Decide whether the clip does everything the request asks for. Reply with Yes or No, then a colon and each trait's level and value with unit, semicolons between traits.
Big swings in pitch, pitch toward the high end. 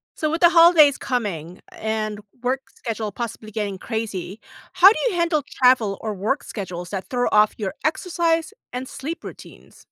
Yes: wide, 6.8 semitones; high, 230 Hz